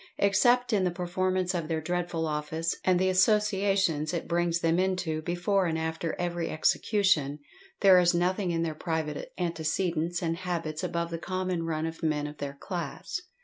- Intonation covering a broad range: No, narrow, 2.5 semitones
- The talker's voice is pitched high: No, medium, 175 Hz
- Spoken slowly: No, average, 170 wpm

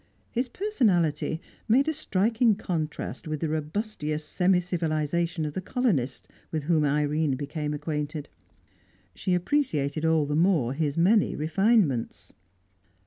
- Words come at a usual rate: No, slow, 125 wpm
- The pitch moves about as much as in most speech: Yes, average, 4.7 semitones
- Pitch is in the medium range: Yes, medium, 160 Hz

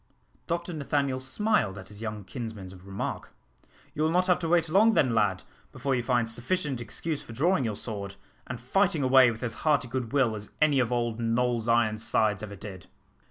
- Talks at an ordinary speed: Yes, average, 190 wpm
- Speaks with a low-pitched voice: Yes, low, 125 Hz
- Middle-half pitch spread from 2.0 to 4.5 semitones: No, wide, 5.5 semitones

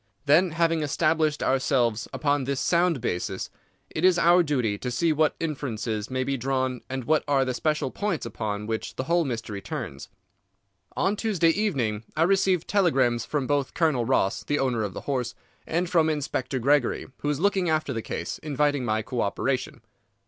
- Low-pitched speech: No, medium, 145 Hz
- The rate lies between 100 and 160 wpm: No, average, 180 wpm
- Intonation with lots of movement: No, average, 4.8 semitones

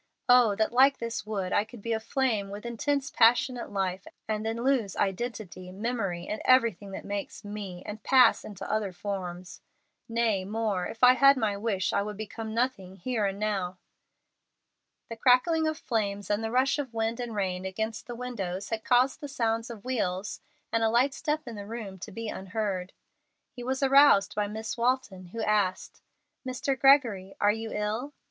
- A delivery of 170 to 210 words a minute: Yes, average, 180 wpm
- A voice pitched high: Yes, high, 220 Hz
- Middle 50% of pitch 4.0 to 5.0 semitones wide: No, average, 3.6 semitones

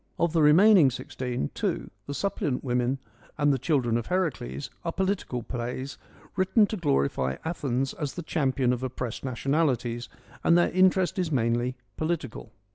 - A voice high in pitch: No, low, 135 Hz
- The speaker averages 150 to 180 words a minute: Yes, average, 155 wpm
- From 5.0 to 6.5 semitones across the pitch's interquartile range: Yes, wide, 5.6 semitones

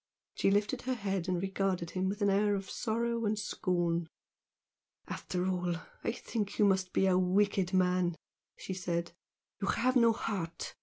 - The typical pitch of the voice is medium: No, high, 195 Hz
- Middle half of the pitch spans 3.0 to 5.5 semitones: No, narrow, 2.4 semitones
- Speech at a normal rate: Yes, average, 165 wpm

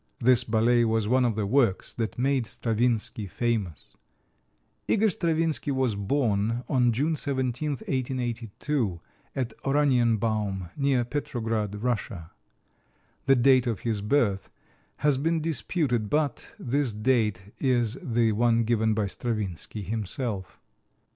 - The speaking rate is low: Yes, slow, 120 wpm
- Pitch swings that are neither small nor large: Yes, average, 3.8 semitones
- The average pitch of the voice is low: Yes, low, 120 Hz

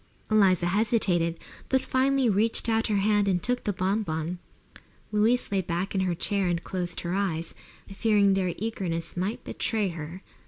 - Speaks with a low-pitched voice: No, high, 195 Hz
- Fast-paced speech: No, average, 165 wpm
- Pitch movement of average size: Yes, average, 3.5 semitones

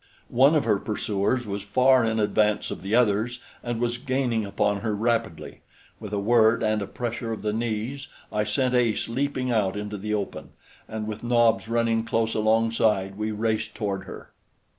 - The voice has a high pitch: No, low, 110 Hz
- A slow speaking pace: No, average, 180 wpm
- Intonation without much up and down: Yes, narrow, 2.2 semitones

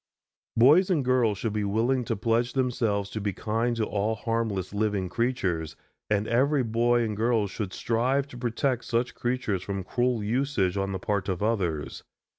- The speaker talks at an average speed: Yes, average, 175 wpm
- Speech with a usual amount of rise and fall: Yes, average, 3.2 semitones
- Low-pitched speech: Yes, low, 115 Hz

